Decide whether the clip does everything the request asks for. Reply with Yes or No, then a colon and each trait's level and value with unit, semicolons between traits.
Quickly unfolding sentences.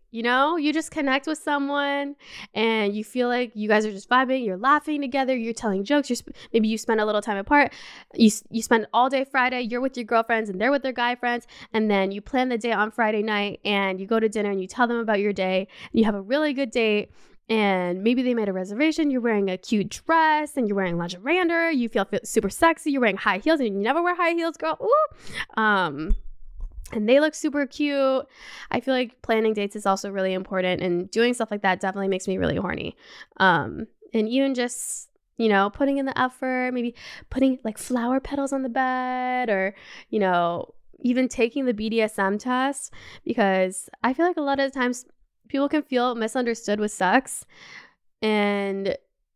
Yes: fast, 210 wpm